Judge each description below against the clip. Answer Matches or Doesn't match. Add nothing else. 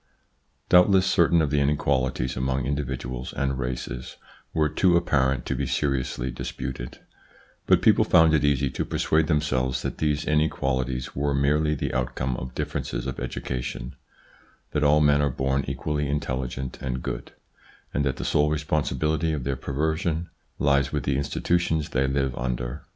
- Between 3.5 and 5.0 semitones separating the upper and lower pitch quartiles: Doesn't match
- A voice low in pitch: Matches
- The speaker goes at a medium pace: Matches